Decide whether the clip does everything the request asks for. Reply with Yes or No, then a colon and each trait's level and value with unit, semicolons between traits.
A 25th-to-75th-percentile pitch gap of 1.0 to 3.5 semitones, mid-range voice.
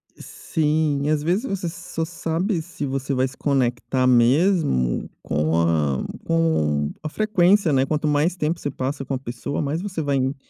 No: average, 4.2 semitones; medium, 145 Hz